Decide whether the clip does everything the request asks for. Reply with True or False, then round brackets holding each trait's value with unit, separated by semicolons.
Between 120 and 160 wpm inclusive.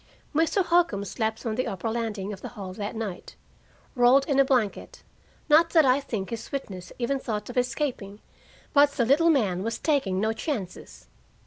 False (180 wpm)